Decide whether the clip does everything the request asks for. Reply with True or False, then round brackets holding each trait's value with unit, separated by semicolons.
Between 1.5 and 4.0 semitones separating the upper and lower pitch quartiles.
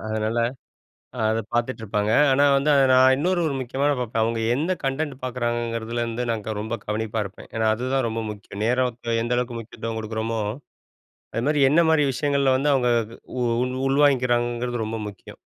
True (2.9 semitones)